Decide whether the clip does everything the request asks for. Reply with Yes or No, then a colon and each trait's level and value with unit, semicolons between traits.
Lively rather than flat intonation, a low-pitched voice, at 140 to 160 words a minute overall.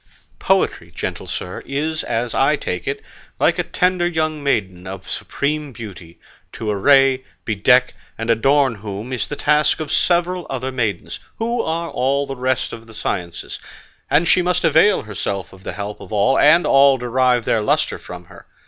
No: wide, 6.0 semitones; low, 130 Hz; average, 175 wpm